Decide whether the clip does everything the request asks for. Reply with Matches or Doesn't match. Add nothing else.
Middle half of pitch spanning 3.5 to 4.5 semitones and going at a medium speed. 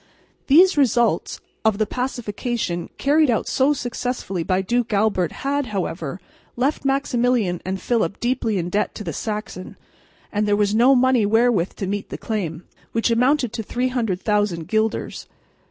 Matches